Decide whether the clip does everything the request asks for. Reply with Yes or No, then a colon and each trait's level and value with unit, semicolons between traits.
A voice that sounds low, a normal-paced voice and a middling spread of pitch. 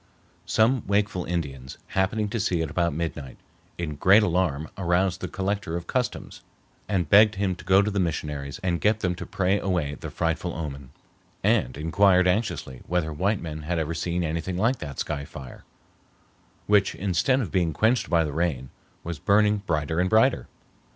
Yes: very low, 90 Hz; average, 175 wpm; average, 4.3 semitones